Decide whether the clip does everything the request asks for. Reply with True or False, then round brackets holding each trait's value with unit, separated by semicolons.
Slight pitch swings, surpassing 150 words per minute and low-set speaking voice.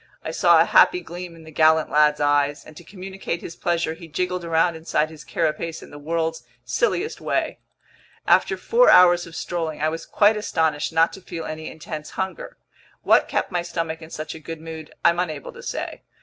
False (2.0 semitones; 200 wpm; 165 Hz)